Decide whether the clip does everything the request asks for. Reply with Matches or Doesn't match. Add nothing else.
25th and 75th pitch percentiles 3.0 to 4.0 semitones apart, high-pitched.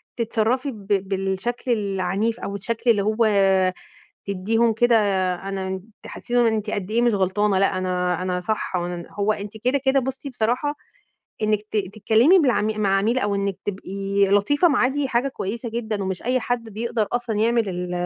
Matches